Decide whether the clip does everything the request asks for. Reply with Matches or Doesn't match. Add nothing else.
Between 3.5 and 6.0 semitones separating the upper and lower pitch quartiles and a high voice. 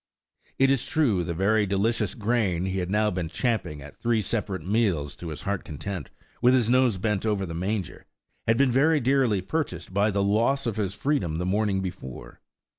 Doesn't match